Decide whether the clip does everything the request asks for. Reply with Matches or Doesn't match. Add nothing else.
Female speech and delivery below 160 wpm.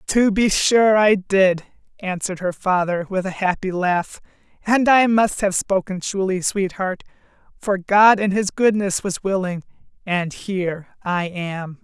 Matches